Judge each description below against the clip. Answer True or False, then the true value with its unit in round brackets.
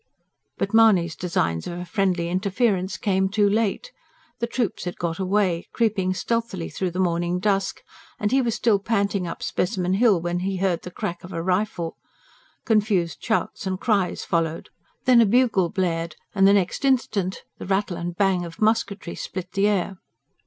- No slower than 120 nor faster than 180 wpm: True (175 wpm)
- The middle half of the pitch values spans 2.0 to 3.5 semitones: True (3.1 semitones)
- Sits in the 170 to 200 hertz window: True (190 Hz)